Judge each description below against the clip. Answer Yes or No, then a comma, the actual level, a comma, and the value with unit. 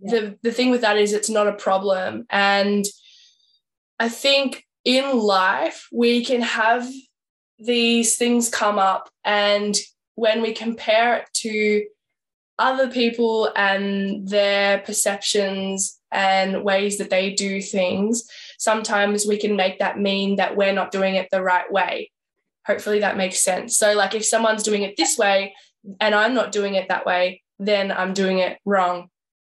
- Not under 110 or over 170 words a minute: Yes, average, 155 wpm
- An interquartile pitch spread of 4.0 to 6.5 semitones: No, average, 2.7 semitones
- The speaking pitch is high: Yes, high, 205 Hz